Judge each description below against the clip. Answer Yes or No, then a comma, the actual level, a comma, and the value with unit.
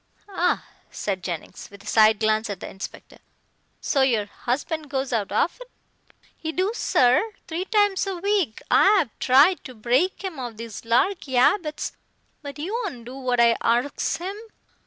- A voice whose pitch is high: Yes, very high, 270 Hz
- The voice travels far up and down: Yes, wide, 8.0 semitones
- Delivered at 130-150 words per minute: No, average, 165 wpm